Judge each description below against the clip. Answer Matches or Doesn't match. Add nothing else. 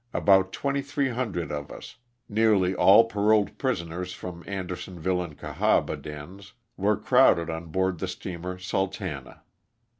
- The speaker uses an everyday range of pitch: Matches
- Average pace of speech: Doesn't match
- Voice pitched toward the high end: Doesn't match